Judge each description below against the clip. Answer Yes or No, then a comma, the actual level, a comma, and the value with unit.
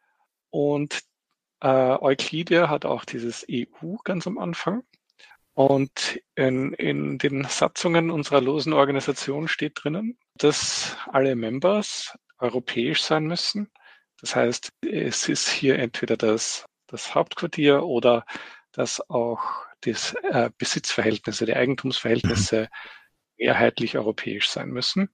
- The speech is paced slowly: Yes, slow, 110 wpm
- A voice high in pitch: No, medium, 140 Hz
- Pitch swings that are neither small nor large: Yes, average, 5.0 semitones